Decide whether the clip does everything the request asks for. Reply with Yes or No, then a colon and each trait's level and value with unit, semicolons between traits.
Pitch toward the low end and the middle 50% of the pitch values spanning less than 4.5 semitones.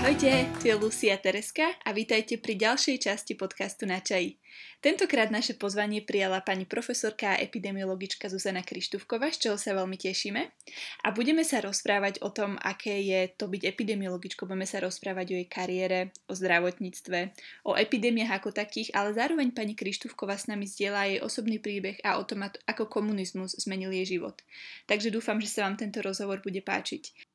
No: high, 200 Hz; narrow, 2.6 semitones